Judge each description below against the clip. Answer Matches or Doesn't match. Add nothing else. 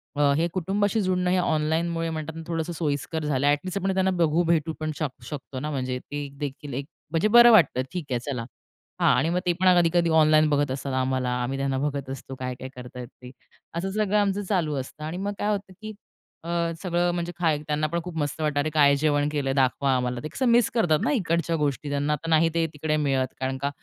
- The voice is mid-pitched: Matches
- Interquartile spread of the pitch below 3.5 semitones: Doesn't match